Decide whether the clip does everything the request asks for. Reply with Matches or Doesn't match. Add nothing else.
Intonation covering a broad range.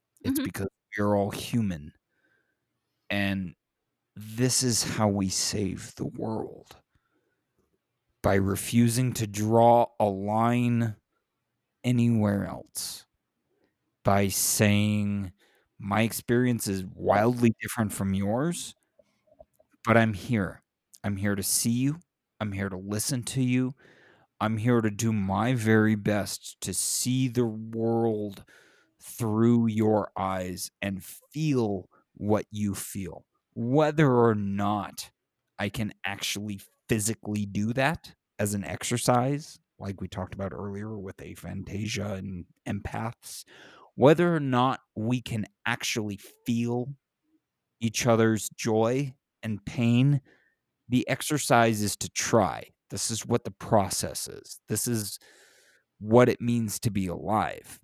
Doesn't match